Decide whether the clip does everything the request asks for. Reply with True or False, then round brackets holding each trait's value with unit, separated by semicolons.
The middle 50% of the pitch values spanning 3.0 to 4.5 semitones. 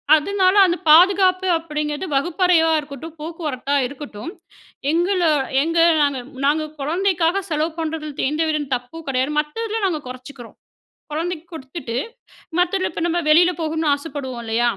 True (3.6 semitones)